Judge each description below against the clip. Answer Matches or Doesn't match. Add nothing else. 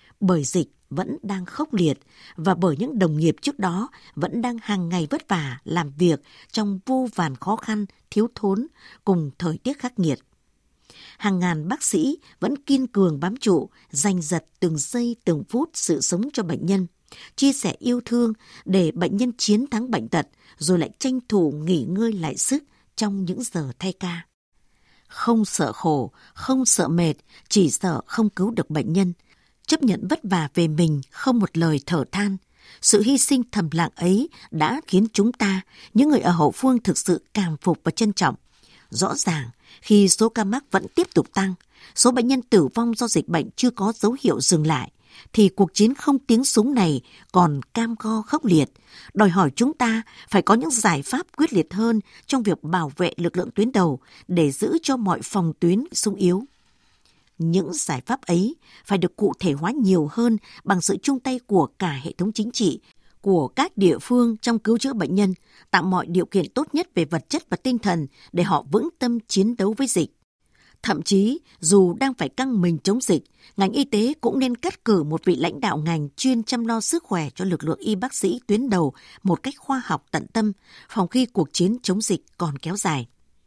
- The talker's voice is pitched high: Matches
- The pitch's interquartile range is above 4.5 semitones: Matches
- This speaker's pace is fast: Doesn't match